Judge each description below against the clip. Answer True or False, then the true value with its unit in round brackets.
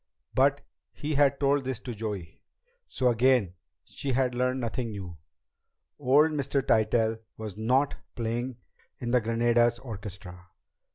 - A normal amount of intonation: True (3.2 semitones)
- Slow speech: True (130 wpm)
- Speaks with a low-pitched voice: True (120 Hz)